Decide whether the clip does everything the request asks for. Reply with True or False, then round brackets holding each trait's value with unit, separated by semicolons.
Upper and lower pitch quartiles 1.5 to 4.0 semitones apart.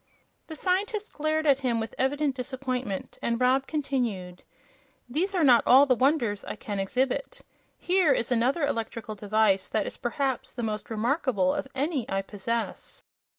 False (4.5 semitones)